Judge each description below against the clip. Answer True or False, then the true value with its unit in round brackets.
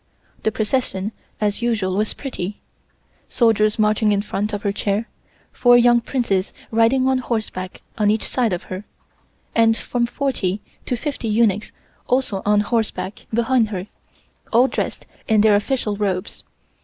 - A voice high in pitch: True (215 Hz)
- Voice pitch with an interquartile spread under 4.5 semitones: True (2.7 semitones)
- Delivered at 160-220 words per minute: False (145 wpm)